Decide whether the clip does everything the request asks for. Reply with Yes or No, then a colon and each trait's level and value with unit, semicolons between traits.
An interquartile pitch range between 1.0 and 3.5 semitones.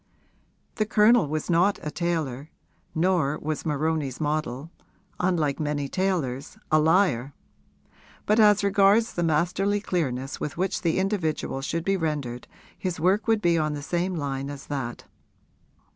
No: average, 4.6 semitones